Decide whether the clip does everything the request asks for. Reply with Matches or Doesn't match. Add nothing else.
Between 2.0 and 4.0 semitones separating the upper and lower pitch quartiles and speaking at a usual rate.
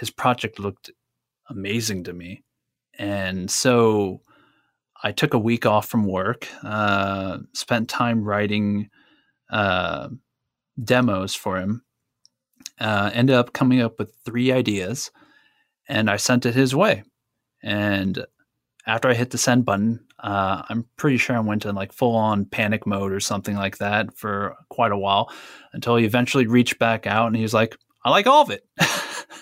Matches